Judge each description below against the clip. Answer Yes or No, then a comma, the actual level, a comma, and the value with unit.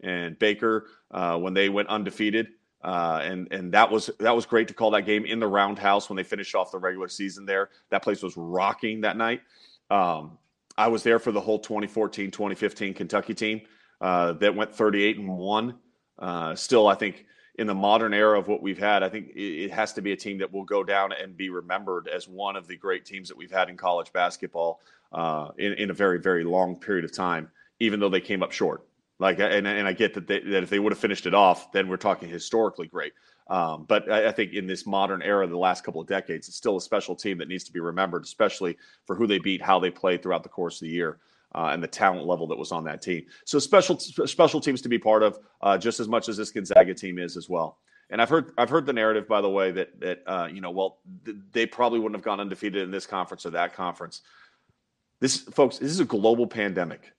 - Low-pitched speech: Yes, low, 100 Hz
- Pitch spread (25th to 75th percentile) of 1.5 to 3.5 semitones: Yes, average, 2.7 semitones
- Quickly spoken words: Yes, fast, 240 wpm